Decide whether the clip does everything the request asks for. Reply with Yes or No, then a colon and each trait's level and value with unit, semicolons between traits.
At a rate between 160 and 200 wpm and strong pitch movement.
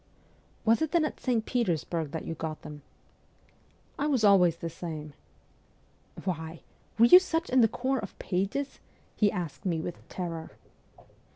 Yes: average, 180 wpm; wide, 7.2 semitones